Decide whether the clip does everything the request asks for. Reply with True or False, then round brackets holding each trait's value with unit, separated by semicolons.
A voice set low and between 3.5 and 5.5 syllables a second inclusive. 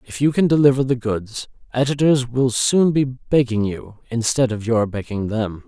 True (125 Hz; 4.6 syllables/s)